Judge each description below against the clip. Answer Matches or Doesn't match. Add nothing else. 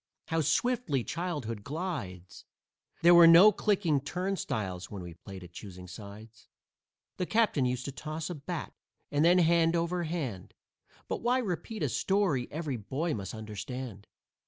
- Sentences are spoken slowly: Doesn't match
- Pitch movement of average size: Doesn't match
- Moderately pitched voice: Matches